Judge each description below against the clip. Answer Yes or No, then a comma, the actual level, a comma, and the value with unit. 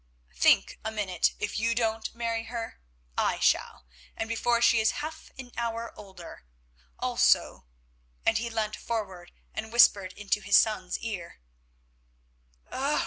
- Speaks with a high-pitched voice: Yes, high, 225 Hz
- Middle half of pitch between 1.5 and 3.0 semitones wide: Yes, narrow, 2.4 semitones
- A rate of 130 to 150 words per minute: Yes, slow, 135 wpm